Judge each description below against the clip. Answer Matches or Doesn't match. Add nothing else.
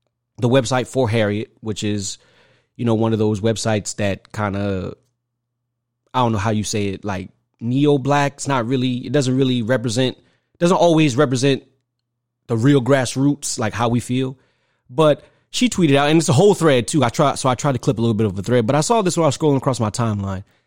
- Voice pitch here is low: Matches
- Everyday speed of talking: Doesn't match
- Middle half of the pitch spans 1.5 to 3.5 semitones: Doesn't match